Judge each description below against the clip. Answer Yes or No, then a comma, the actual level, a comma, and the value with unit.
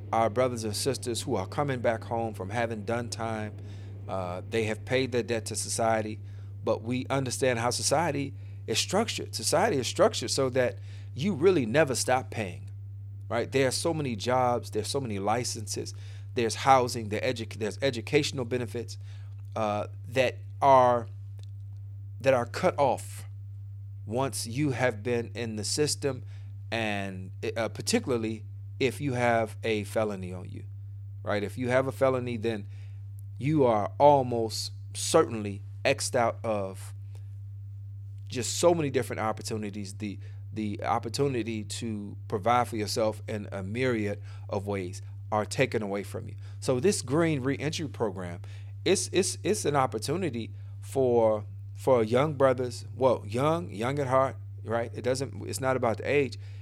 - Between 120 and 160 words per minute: Yes, average, 150 wpm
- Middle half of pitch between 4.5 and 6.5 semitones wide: No, average, 3.8 semitones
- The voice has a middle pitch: No, low, 110 Hz